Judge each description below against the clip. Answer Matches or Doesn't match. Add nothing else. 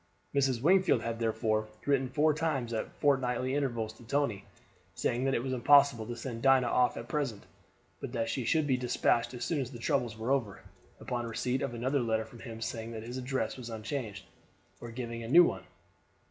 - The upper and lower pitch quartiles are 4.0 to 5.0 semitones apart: Doesn't match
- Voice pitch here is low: Matches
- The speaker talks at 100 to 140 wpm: Doesn't match